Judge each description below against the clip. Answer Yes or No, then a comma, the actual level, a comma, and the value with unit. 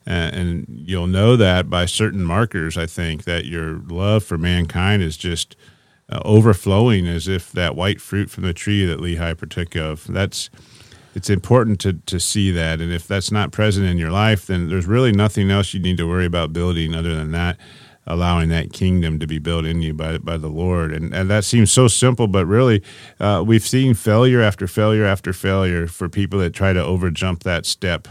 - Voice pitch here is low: Yes, very low, 90 Hz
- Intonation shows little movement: No, average, 3.4 semitones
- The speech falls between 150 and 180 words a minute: No, average, 200 wpm